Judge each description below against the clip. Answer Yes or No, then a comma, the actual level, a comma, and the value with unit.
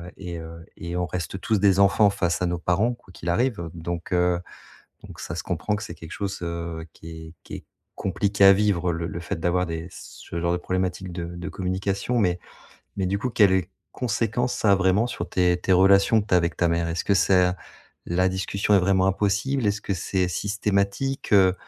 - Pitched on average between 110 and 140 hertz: No, very low, 95 Hz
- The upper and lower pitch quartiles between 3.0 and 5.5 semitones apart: No, narrow, 2.5 semitones